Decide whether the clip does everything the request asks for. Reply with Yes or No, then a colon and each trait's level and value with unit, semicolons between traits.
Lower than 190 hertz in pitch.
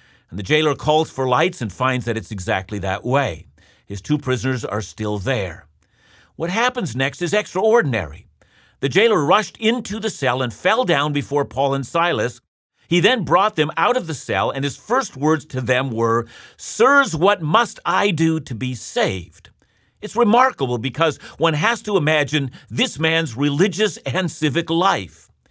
Yes: medium, 140 Hz